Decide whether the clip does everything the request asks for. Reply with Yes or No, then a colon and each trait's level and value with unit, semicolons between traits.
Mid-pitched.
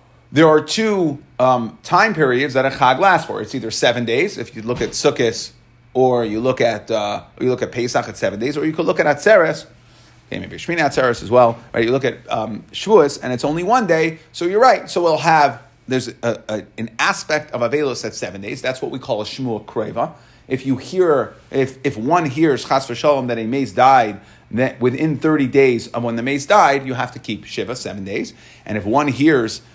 No: low, 130 Hz